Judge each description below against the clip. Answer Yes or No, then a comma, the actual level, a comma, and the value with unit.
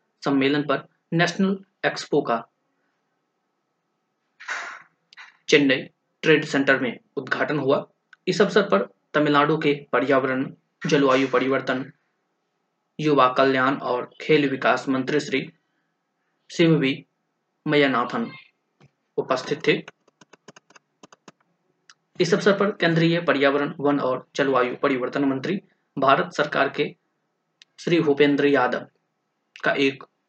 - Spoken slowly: Yes, slow, 90 wpm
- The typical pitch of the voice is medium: Yes, medium, 145 Hz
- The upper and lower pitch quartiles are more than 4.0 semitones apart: No, average, 3.7 semitones